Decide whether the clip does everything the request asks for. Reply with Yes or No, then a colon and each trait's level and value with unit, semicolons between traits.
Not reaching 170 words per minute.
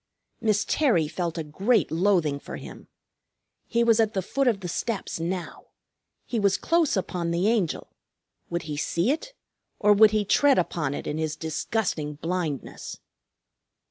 Yes: average, 160 wpm